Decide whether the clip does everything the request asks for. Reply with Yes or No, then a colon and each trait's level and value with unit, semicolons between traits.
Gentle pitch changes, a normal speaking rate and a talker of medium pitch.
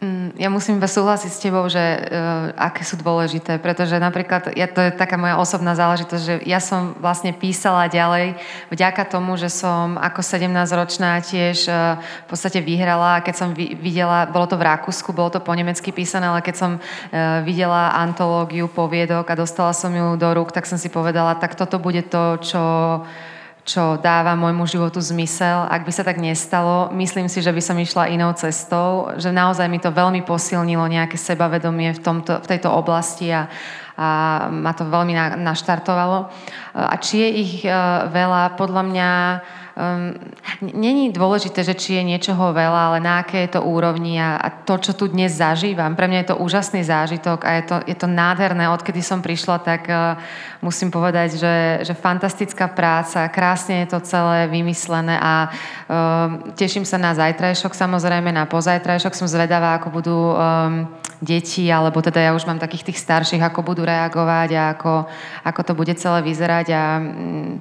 No: narrow, 1.4 semitones; fast, 170 wpm; medium, 175 Hz